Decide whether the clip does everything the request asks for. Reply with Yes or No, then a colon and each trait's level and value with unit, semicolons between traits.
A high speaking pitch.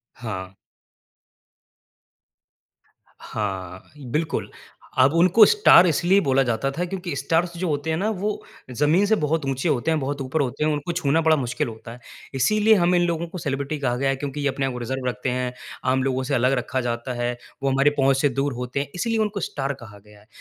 No: medium, 140 Hz